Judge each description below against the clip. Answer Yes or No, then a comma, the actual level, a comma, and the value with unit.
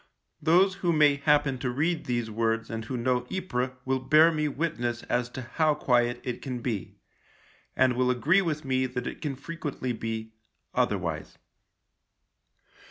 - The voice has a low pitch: Yes, low, 130 Hz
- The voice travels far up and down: No, average, 3.9 semitones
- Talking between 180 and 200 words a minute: No, average, 165 wpm